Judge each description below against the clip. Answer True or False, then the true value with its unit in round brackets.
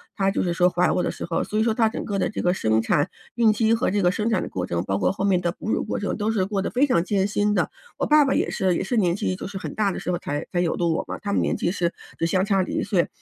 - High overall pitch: True (195 Hz)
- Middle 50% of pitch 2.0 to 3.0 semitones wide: False (3.4 semitones)